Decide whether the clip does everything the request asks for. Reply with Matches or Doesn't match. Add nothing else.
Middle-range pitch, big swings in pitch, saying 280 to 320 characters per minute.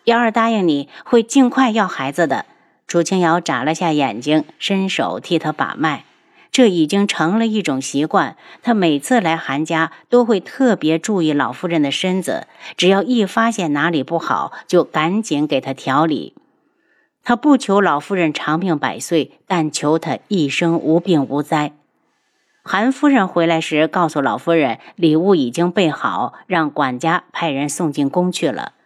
Doesn't match